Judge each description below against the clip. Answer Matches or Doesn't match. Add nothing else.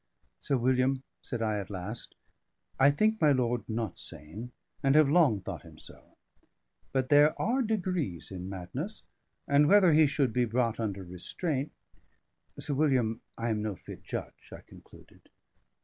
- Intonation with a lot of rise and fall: Matches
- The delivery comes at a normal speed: Matches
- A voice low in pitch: Matches